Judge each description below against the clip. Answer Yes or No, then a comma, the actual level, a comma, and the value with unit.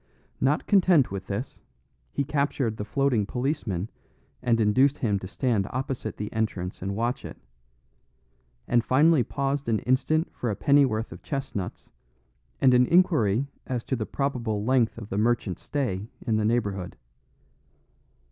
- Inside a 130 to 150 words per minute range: Yes, average, 145 wpm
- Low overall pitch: Yes, low, 120 Hz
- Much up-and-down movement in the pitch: No, average, 4.6 semitones